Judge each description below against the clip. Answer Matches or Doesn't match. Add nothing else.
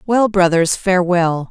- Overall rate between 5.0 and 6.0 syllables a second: Doesn't match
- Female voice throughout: Matches